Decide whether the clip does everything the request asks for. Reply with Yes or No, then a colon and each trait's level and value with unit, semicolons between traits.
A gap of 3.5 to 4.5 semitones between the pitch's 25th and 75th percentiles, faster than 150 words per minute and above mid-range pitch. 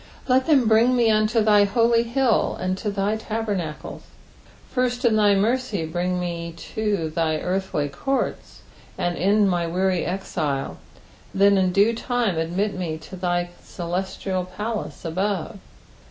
No: average, 4.0 semitones; average, 145 wpm; high, 195 Hz